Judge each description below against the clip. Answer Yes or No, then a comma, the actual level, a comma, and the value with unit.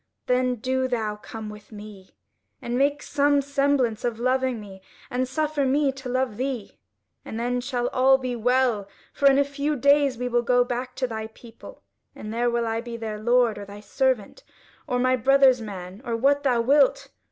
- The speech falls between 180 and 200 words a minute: Yes, average, 190 wpm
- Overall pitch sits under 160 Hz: No, very high, 250 Hz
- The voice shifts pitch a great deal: No, average, 3.0 semitones